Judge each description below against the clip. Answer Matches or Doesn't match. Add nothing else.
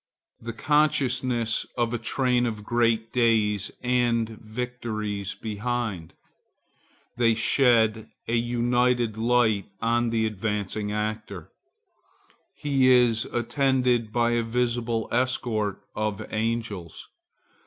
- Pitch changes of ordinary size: Doesn't match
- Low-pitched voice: Matches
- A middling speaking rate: Doesn't match